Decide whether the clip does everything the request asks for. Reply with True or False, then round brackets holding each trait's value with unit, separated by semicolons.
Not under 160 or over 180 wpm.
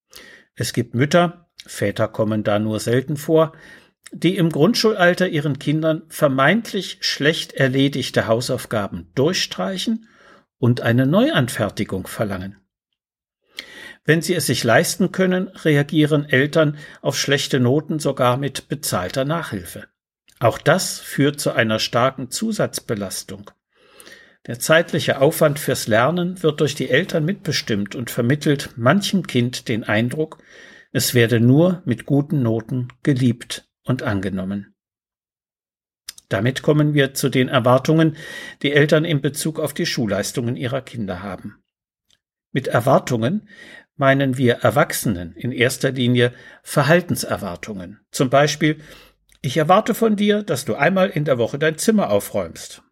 False (125 wpm)